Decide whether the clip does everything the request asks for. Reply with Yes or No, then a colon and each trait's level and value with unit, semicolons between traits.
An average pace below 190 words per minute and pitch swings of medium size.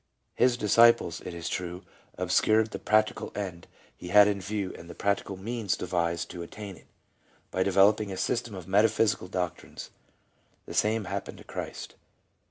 Yes: average, 160 wpm; average, 3.0 semitones